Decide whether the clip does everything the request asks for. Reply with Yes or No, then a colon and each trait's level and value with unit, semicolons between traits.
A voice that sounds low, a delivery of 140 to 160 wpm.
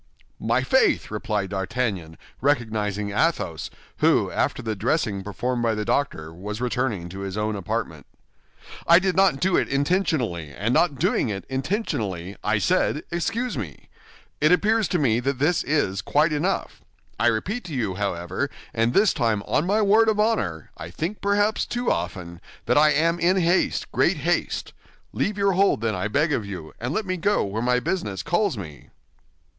No: low, 125 Hz; average, 170 wpm